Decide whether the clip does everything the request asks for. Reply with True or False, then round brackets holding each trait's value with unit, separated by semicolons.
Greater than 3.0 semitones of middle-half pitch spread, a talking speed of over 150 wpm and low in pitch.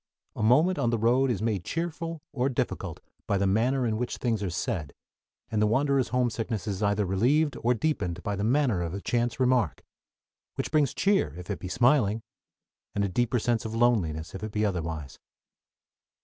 True (4.3 semitones; 190 wpm; 115 Hz)